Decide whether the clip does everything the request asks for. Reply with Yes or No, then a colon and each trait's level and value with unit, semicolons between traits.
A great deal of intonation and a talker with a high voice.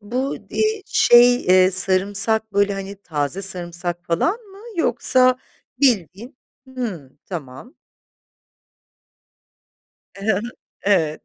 Yes: wide, 5.9 semitones; high, 200 Hz